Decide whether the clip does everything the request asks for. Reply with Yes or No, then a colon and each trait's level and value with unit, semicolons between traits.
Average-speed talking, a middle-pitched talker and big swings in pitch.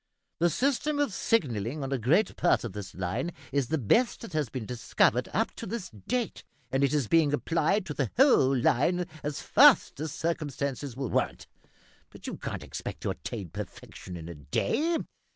Yes: average, 185 wpm; medium, 145 Hz; wide, 6.7 semitones